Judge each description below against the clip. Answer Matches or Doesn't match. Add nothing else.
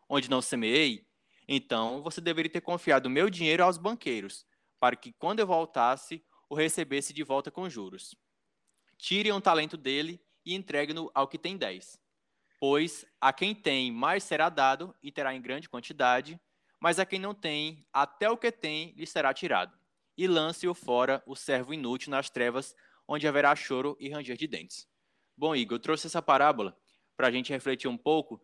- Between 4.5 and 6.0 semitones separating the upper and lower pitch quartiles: Doesn't match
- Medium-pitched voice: Matches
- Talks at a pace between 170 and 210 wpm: Matches